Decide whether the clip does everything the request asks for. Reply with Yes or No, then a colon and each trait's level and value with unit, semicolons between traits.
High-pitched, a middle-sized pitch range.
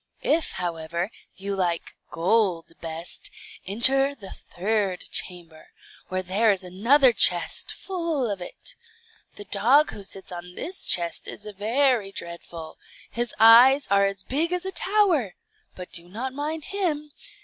No: high, 205 Hz; wide, 7.3 semitones